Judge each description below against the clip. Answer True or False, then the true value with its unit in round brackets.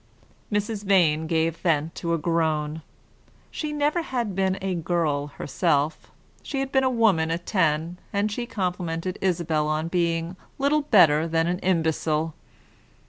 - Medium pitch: True (170 Hz)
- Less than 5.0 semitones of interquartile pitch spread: True (3.9 semitones)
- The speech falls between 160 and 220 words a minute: False (145 wpm)